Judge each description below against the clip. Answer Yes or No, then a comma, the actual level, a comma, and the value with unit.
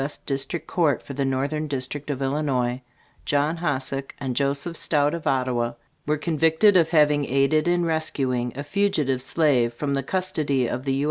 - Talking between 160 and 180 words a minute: Yes, average, 175 wpm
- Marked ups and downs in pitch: No, average, 2.7 semitones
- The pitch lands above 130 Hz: Yes, medium, 140 Hz